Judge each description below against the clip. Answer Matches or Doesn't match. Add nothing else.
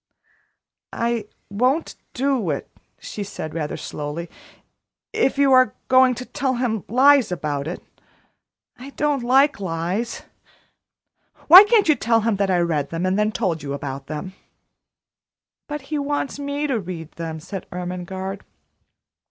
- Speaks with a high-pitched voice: Matches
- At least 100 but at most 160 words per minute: Matches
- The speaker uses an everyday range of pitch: Doesn't match